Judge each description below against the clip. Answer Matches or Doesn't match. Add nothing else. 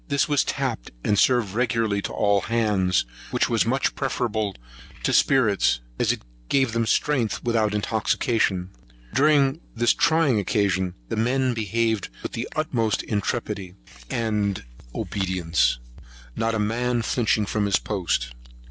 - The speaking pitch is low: Matches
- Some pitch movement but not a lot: Matches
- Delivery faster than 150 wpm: Doesn't match